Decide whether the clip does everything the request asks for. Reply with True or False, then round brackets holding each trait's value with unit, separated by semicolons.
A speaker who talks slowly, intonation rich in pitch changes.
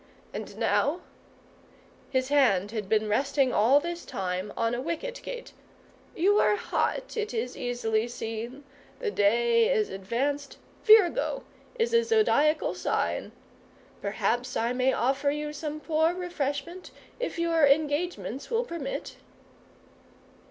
True (130 wpm; 6.6 semitones)